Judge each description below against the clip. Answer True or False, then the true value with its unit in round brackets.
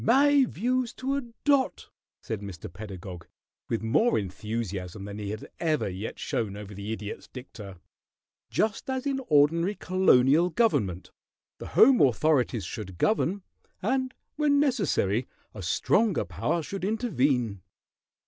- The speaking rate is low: True (130 wpm)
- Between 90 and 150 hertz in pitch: True (135 Hz)